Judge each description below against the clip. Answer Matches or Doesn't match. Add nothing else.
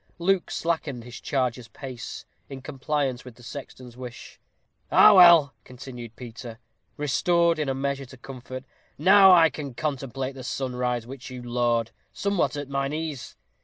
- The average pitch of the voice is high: Doesn't match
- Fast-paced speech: Doesn't match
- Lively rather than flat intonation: Doesn't match